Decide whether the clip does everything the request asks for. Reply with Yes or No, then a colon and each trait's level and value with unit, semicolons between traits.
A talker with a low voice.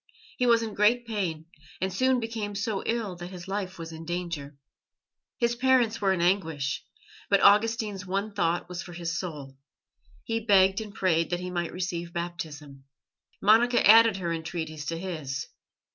No: medium, 185 Hz